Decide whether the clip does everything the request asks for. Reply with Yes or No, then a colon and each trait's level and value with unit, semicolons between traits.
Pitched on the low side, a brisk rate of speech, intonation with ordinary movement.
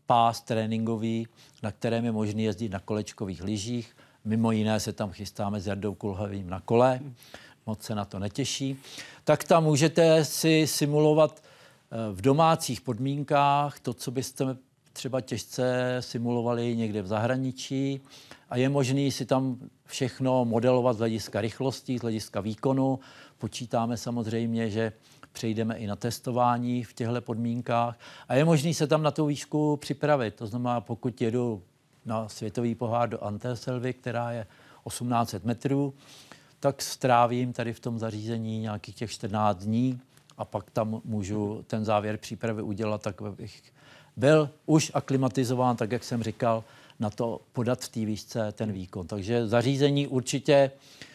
No: low, 120 Hz; average, 145 wpm; average, 3.4 semitones